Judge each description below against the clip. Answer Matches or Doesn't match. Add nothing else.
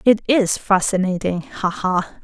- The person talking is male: Doesn't match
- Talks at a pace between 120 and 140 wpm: Matches